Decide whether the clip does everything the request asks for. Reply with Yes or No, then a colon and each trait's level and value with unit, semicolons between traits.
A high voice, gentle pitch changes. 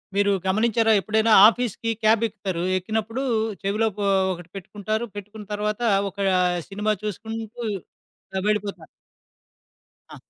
Yes: high, 210 Hz; narrow, 1.9 semitones